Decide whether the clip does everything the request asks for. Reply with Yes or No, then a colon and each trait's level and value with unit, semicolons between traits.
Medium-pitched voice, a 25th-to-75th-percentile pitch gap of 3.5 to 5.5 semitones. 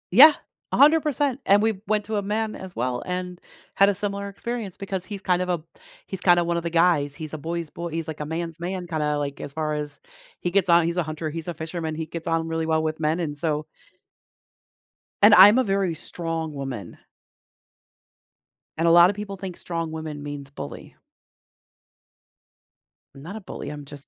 Yes: medium, 170 Hz; average, 3.8 semitones